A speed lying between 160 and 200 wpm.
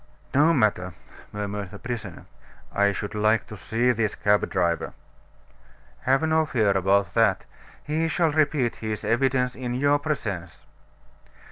No: slow, 135 wpm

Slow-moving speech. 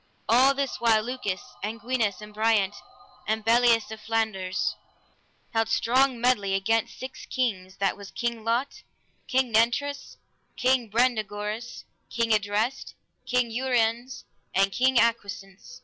Yes: slow, 125 wpm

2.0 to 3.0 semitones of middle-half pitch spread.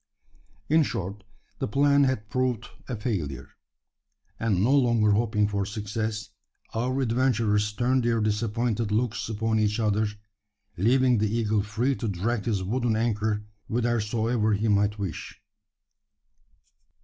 Yes: narrow, 2.4 semitones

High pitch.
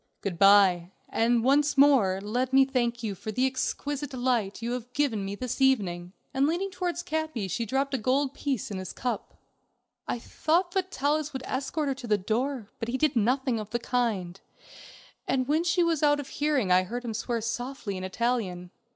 Yes: very high, 250 Hz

